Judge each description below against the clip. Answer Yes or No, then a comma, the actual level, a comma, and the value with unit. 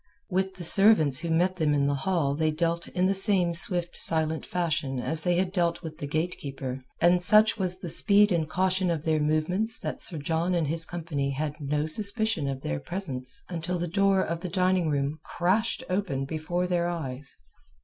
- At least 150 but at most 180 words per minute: No, average, 195 wpm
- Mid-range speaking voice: Yes, medium, 170 Hz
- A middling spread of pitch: Yes, average, 3.3 semitones